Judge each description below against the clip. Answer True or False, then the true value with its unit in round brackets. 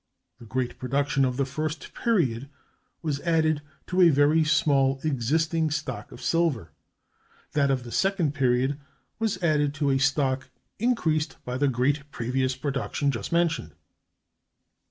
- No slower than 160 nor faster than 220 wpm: False (140 wpm)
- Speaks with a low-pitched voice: False (145 Hz)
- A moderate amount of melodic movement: True (3.2 semitones)